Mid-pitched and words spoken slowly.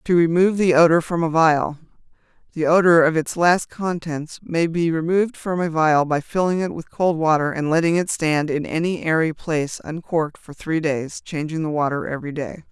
No: medium, 160 Hz; average, 195 wpm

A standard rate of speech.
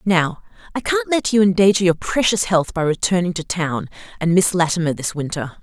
Yes: average, 190 wpm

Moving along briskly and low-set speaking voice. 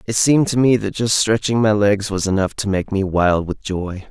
Yes: fast, 250 wpm; low, 105 Hz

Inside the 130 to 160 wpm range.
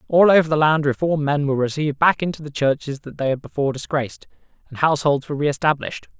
No: fast, 205 wpm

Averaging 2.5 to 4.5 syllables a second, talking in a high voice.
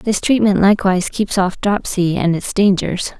No: 4.9 syllables/s; high, 195 Hz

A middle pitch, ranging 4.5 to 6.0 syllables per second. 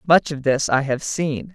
No: medium, 145 Hz; 4.3 syllables/s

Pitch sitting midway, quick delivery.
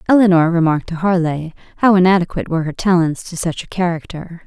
No: medium, 175 Hz; average, 175 wpm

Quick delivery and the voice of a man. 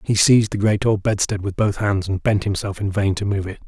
Yes: fast, 280 wpm; male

